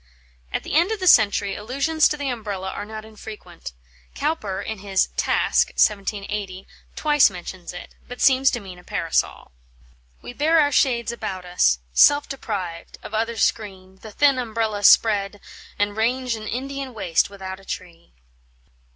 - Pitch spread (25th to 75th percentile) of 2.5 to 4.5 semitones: No, average, 5.0 semitones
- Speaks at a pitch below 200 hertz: No, high, 215 Hz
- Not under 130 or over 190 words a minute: Yes, average, 160 wpm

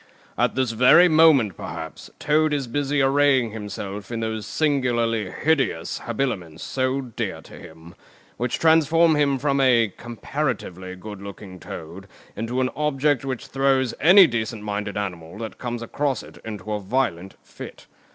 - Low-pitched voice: Yes, low, 120 Hz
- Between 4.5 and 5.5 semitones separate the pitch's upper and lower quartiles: Yes, average, 5.1 semitones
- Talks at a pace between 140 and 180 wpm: Yes, average, 150 wpm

